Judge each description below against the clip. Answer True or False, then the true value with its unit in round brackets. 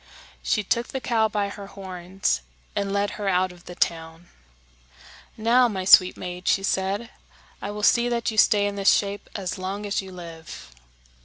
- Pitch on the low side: False (200 Hz)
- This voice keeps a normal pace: True (180 wpm)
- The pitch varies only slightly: True (2.3 semitones)